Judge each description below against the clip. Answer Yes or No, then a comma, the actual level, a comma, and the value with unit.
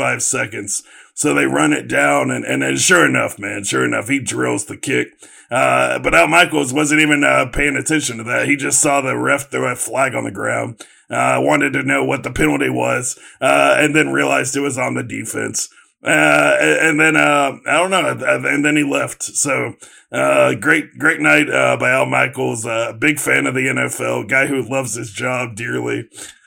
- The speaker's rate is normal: No, fast, 210 wpm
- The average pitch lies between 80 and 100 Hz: No, low, 130 Hz